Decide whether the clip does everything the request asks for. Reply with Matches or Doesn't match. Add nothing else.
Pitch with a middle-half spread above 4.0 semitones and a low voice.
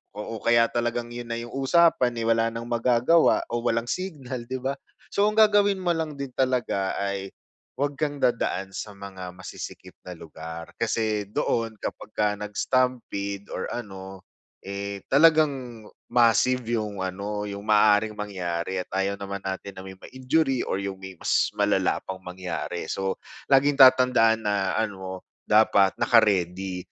Matches